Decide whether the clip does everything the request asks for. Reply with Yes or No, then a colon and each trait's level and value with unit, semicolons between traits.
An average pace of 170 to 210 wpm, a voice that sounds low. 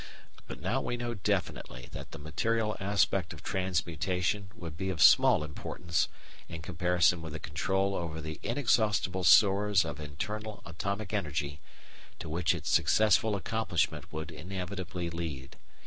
No: average, 140 wpm; very low, 90 Hz